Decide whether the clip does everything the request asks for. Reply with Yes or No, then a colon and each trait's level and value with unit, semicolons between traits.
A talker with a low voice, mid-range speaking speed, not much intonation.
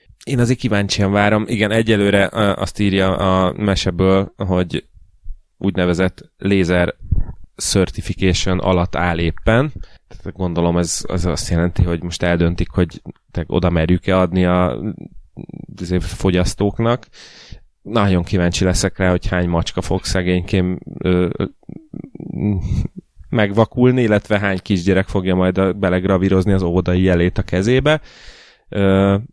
Yes: very low, 95 Hz; average, 115 wpm; narrow, 2.0 semitones